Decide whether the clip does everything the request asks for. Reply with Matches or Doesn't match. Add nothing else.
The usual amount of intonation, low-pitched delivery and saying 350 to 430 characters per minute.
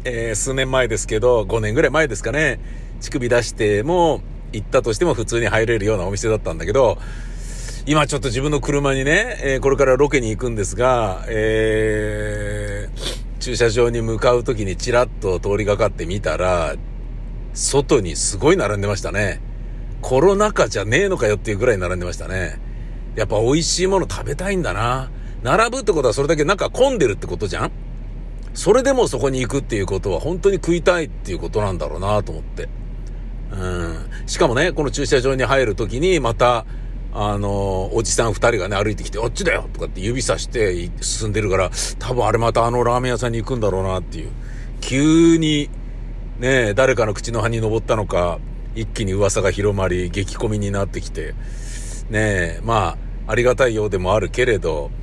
Matches